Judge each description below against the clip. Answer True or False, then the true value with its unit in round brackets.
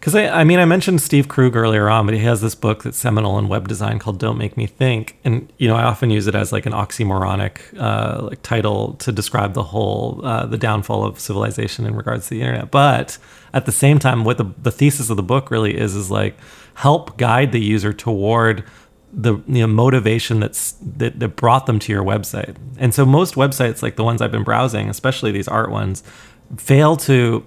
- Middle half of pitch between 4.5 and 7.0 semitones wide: False (3.1 semitones)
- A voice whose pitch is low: True (115 Hz)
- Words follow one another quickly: True (225 wpm)